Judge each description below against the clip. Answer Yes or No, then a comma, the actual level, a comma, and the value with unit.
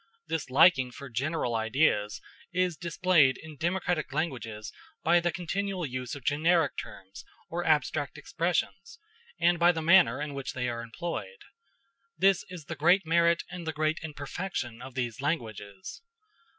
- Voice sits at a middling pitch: Yes, medium, 155 Hz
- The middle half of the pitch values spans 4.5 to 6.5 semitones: Yes, average, 5.2 semitones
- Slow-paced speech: No, average, 150 wpm